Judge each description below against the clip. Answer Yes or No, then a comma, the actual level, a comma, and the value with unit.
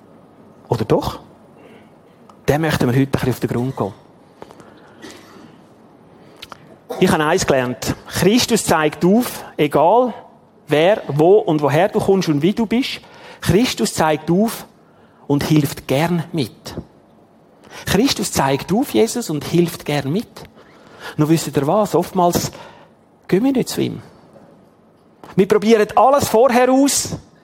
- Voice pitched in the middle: Yes, medium, 170 Hz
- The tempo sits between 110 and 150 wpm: Yes, average, 130 wpm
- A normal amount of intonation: No, wide, 6.7 semitones